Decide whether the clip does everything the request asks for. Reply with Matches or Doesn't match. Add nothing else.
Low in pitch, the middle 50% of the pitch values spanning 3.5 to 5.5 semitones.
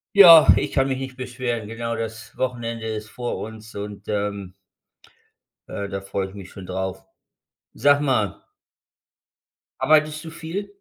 Matches